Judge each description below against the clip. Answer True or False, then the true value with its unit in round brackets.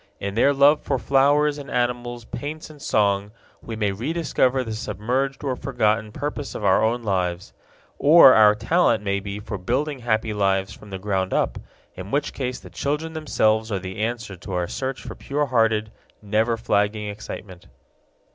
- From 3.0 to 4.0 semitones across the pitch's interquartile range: False (4.9 semitones)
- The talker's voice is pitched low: True (110 Hz)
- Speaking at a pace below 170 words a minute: False (175 wpm)